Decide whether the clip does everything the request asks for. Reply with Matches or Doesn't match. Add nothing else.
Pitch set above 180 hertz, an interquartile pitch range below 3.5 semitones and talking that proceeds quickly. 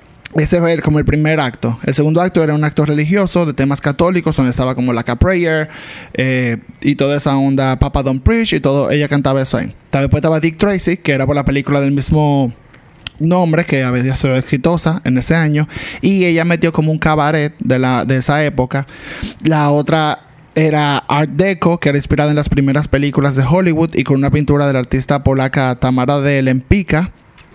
Doesn't match